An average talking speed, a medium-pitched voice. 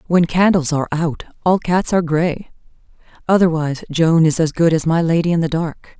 Yes: average, 190 wpm; medium, 165 Hz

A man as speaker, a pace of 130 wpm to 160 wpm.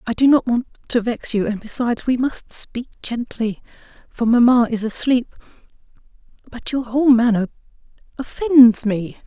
No: female; average, 150 wpm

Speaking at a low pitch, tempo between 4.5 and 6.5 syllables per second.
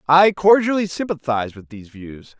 No: medium, 155 Hz; 5.4 syllables/s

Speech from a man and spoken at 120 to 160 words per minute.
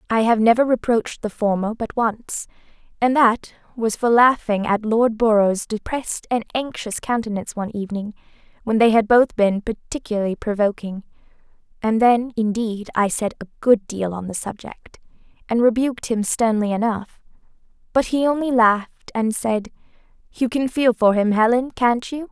No: female; average, 155 wpm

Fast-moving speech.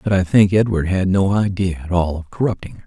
Yes: fast, 250 wpm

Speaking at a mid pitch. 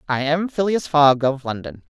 Yes: medium, 150 Hz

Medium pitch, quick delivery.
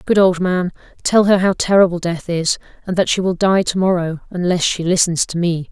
Yes: medium, 180 Hz; fast, 220 wpm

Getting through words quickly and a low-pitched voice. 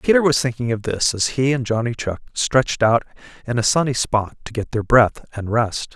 Yes: fast, 220 wpm; low, 120 Hz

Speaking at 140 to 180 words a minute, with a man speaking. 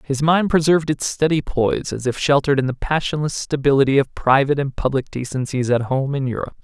No: average, 200 wpm; male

